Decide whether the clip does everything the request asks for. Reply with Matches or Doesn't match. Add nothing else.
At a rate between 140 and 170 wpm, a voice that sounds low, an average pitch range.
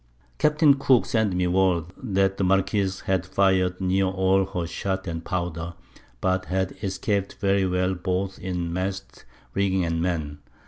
Doesn't match